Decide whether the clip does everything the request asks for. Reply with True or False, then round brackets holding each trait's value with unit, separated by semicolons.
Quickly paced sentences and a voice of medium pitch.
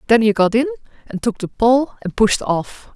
False (225 wpm; 230 Hz)